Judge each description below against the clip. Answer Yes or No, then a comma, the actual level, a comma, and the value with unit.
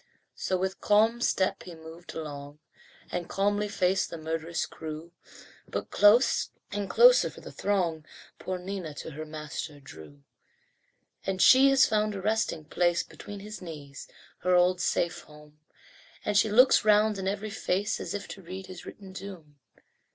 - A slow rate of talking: No, average, 160 wpm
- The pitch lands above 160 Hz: Yes, medium, 185 Hz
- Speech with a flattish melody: No, average, 4.3 semitones